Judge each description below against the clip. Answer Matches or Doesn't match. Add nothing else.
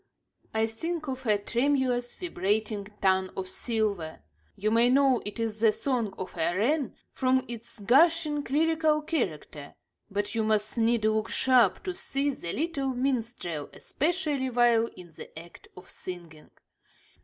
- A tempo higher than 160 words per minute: Doesn't match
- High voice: Matches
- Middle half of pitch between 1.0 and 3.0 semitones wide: Doesn't match